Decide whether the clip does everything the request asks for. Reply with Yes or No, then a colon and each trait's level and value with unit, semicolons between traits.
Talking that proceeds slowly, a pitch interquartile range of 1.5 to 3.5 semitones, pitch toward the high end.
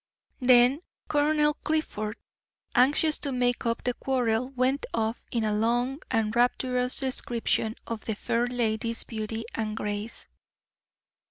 Yes: slow, 125 wpm; narrow, 2.5 semitones; high, 240 Hz